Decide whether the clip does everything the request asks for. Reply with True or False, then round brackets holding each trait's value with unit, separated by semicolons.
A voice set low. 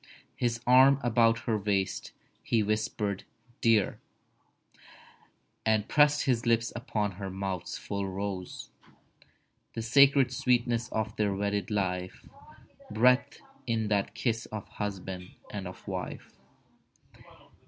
True (110 Hz)